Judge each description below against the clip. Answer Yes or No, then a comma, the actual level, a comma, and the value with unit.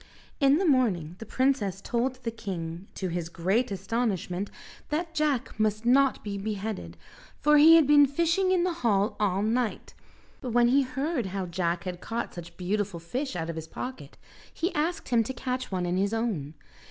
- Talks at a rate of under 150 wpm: No, average, 185 wpm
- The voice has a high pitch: Yes, high, 225 Hz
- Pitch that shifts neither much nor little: No, wide, 6.2 semitones